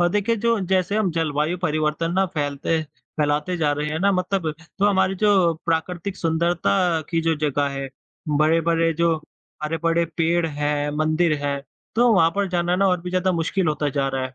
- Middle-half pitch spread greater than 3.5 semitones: No, average, 3.1 semitones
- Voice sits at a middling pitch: Yes, medium, 165 Hz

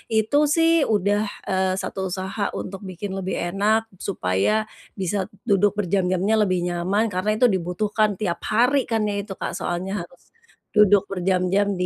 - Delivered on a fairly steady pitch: Yes, narrow, 2.3 semitones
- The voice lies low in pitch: No, high, 195 Hz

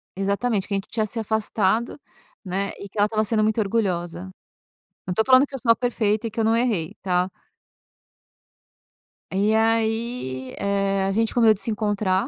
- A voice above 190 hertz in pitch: Yes, high, 215 Hz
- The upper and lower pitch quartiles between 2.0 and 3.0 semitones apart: Yes, narrow, 2.6 semitones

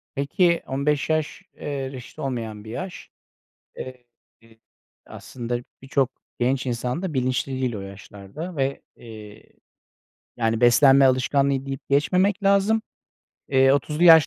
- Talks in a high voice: No, low, 135 Hz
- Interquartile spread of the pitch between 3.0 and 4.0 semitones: Yes, average, 3.7 semitones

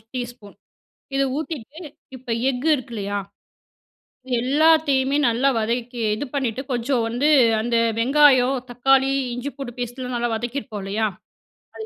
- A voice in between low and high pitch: No, very high, 250 Hz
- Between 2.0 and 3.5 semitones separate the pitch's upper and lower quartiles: Yes, average, 2.8 semitones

